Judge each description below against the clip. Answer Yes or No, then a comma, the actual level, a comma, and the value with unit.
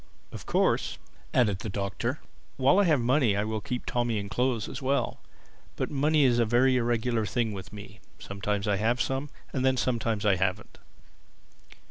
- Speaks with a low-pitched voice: Yes, low, 120 Hz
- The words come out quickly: No, average, 175 wpm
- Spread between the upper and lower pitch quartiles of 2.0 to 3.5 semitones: No, average, 3.9 semitones